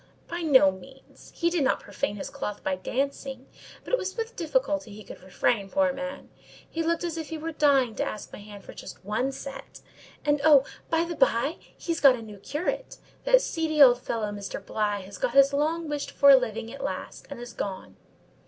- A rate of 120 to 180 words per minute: No, average, 200 wpm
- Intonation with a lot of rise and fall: Yes, wide, 6.5 semitones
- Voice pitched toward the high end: Yes, very high, 275 Hz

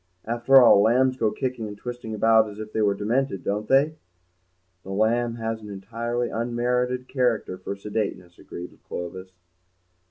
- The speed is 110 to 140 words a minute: No, average, 155 wpm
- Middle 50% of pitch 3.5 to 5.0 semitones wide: No, average, 3.0 semitones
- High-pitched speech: No, low, 115 Hz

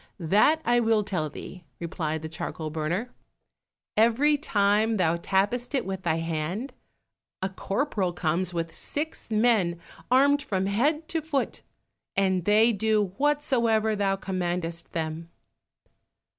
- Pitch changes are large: Yes, wide, 5.7 semitones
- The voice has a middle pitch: No, high, 200 Hz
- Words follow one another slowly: Yes, slow, 130 wpm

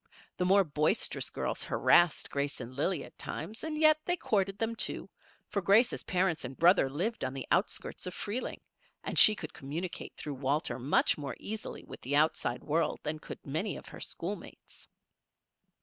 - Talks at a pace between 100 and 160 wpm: No, average, 175 wpm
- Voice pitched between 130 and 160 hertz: No, medium, 170 Hz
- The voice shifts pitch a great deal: Yes, wide, 6.1 semitones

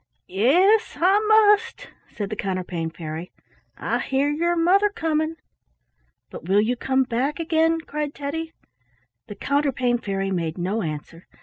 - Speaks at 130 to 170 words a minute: Yes, slow, 135 wpm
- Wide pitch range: Yes, wide, 9.0 semitones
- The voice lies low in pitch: No, very high, 275 Hz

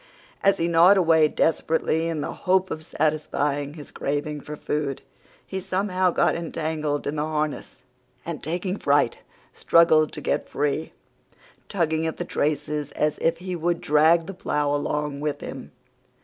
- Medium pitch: Yes, medium, 155 Hz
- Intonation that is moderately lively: No, narrow, 2.3 semitones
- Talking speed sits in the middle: Yes, average, 155 wpm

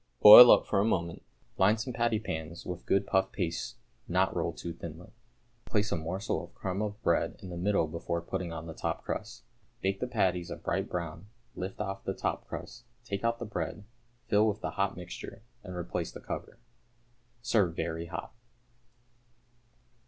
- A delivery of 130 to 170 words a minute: No, average, 180 wpm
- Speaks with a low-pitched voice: Yes, very low, 95 Hz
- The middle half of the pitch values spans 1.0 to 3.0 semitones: No, average, 3.6 semitones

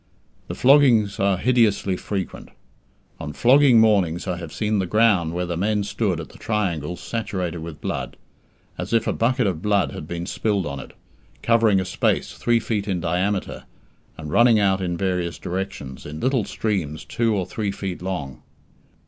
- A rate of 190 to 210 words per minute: No, average, 175 wpm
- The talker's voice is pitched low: Yes, very low, 95 Hz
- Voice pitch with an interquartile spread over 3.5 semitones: Yes, average, 4.0 semitones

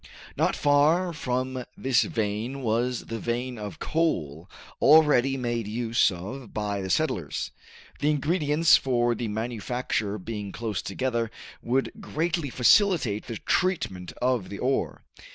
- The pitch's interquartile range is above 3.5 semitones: Yes, average, 4.7 semitones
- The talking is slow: Yes, slow, 130 wpm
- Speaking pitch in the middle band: No, low, 120 Hz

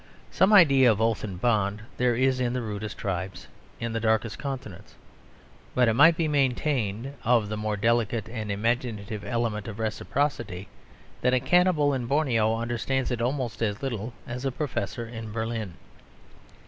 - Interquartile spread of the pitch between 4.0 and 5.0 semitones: No, average, 3.2 semitones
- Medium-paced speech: Yes, average, 160 wpm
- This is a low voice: Yes, low, 115 Hz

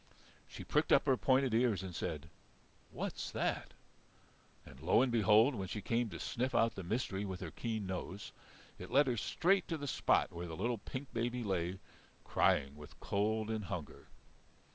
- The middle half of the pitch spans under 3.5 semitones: No, average, 4.9 semitones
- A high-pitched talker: No, low, 110 Hz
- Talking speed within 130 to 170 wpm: No, average, 180 wpm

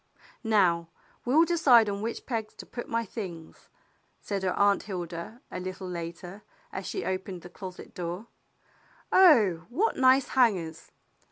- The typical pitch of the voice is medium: No, high, 200 Hz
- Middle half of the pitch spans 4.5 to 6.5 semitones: Yes, average, 4.9 semitones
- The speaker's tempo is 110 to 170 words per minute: Yes, average, 145 wpm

